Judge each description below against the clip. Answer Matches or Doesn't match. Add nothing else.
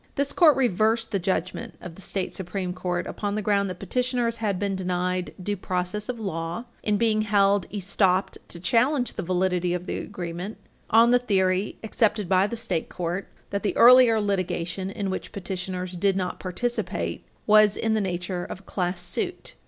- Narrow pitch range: Doesn't match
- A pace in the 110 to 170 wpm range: Doesn't match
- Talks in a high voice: Matches